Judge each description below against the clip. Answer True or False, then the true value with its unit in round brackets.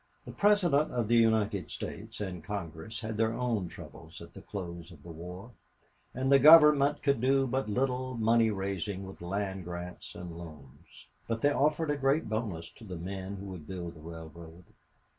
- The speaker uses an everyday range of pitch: False (6.5 semitones)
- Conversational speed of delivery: True (180 wpm)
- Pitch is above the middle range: False (105 Hz)